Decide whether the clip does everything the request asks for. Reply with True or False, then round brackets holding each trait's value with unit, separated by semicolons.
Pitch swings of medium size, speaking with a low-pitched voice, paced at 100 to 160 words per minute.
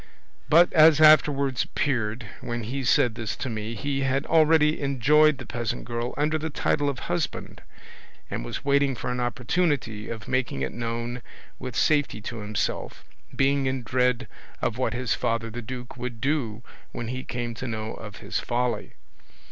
False (3.3 semitones; 125 Hz; 170 wpm)